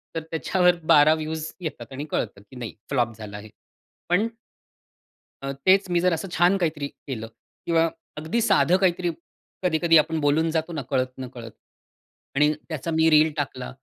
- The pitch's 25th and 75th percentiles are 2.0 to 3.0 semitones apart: No, average, 4.0 semitones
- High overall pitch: No, medium, 155 Hz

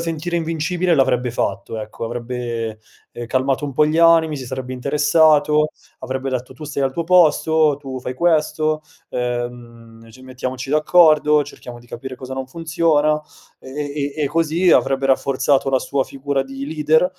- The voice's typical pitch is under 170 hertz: Yes, medium, 140 Hz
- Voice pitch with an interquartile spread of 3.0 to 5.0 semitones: Yes, average, 3.4 semitones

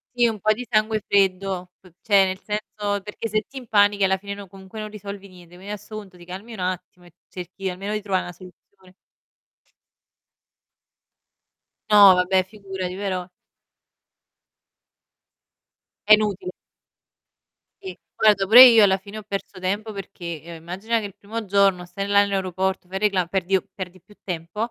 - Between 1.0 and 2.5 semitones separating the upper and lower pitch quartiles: Yes, narrow, 2.1 semitones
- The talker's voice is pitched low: No, high, 195 Hz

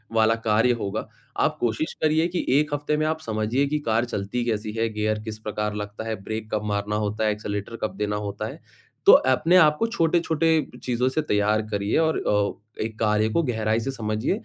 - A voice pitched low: Yes, low, 110 Hz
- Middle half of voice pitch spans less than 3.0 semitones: No, average, 4.6 semitones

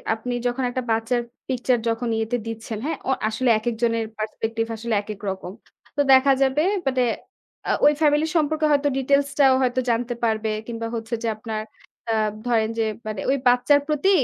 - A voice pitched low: No, high, 240 Hz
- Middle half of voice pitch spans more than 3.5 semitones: No, average, 3.2 semitones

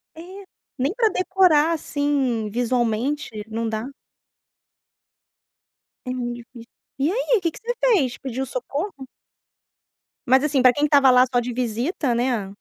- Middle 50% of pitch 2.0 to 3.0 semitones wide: No, average, 3.9 semitones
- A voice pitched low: No, very high, 260 Hz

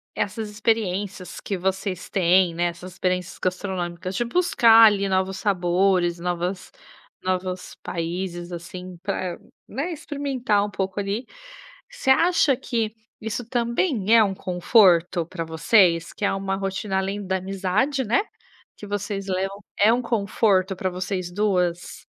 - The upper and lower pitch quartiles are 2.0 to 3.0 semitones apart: Yes, average, 2.7 semitones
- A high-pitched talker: Yes, high, 195 Hz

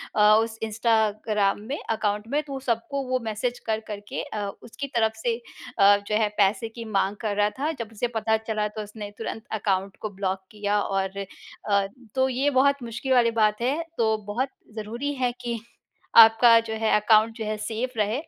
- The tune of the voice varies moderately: No, narrow, 2.3 semitones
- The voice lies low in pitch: No, high, 220 Hz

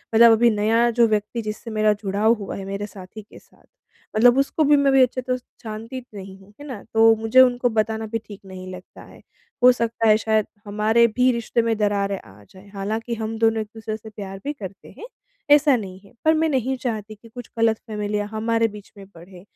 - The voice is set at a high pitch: Yes, high, 220 Hz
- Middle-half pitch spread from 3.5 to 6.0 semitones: No, narrow, 2.4 semitones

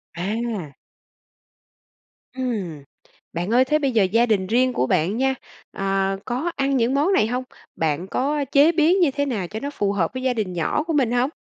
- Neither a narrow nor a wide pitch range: No, wide, 6.0 semitones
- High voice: Yes, high, 240 Hz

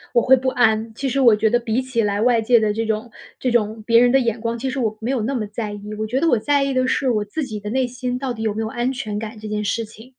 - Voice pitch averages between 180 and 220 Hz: No, high, 230 Hz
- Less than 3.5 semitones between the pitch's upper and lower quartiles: Yes, average, 2.8 semitones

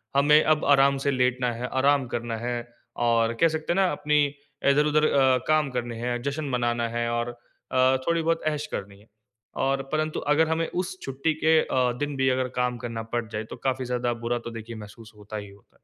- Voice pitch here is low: Yes, low, 130 Hz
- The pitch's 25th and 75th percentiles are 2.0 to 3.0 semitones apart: No, average, 4.1 semitones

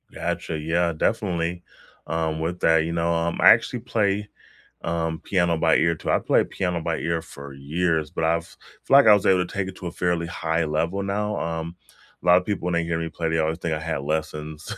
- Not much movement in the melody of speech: Yes, narrow, 1.9 semitones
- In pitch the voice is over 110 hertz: No, very low, 85 Hz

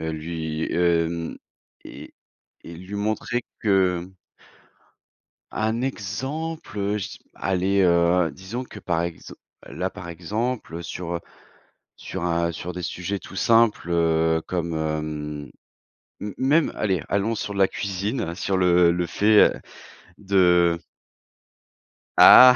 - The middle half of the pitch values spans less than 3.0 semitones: No, average, 3.6 semitones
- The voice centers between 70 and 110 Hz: Yes, very low, 90 Hz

